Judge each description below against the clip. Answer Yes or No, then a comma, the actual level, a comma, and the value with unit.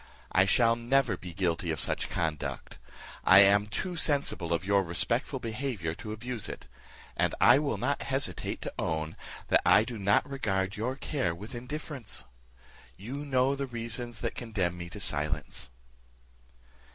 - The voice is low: Yes, low, 105 Hz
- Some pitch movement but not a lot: No, wide, 6.2 semitones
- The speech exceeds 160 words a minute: No, average, 155 wpm